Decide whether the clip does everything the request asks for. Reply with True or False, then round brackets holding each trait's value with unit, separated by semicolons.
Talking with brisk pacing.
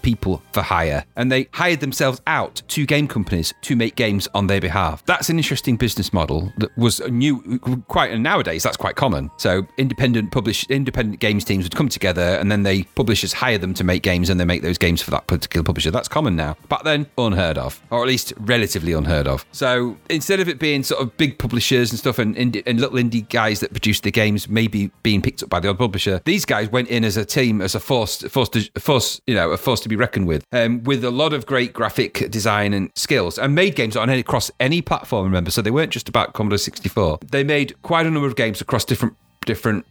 True (235 wpm)